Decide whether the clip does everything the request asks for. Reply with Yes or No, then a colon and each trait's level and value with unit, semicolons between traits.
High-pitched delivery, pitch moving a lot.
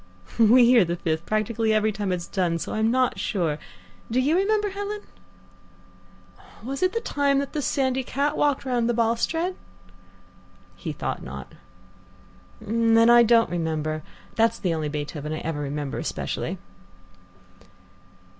Yes: high, 230 Hz; wide, 7.7 semitones